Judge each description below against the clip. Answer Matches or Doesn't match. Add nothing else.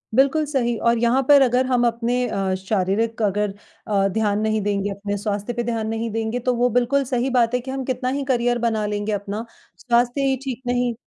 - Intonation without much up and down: Doesn't match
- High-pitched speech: Matches